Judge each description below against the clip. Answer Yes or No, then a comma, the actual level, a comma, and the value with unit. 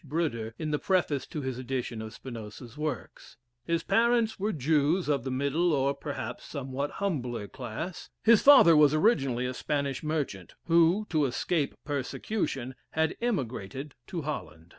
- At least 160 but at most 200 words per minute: No, average, 150 wpm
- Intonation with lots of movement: No, average, 4.6 semitones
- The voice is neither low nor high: Yes, medium, 145 Hz